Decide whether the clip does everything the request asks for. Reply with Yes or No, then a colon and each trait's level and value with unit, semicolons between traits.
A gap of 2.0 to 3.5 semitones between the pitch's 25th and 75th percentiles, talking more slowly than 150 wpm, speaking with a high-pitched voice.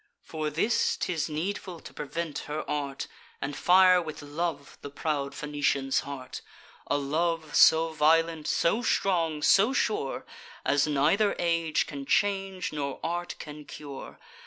No: average, 3.2 semitones; slow, 135 wpm; medium, 155 Hz